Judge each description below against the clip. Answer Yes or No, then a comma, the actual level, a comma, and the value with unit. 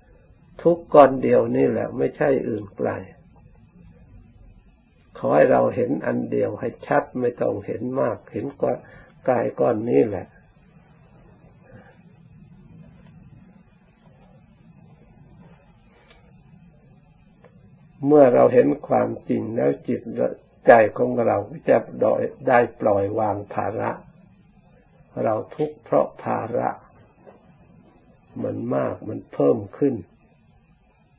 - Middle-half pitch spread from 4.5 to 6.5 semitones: Yes, wide, 5.4 semitones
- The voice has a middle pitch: Yes, medium, 150 Hz